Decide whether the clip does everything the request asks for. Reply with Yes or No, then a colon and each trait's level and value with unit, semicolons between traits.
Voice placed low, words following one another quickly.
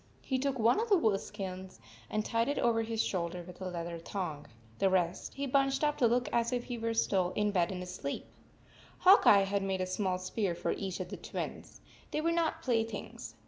No: high, 210 Hz; fast, 225 wpm